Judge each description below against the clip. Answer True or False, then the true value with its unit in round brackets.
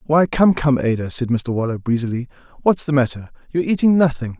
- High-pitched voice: False (135 Hz)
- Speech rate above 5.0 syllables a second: True (5.9 syllables/s)